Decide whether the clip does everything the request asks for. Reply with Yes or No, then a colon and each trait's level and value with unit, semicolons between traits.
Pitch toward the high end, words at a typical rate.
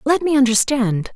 Yes: very high, 255 Hz; average, 155 wpm